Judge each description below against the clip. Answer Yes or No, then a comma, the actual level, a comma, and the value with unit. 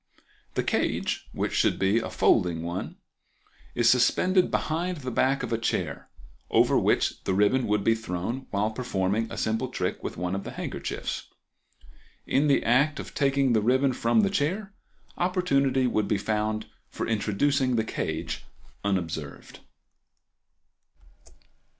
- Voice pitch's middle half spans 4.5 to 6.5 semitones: Yes, average, 5.1 semitones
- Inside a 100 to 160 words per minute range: Yes, average, 145 wpm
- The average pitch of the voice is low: Yes, low, 115 Hz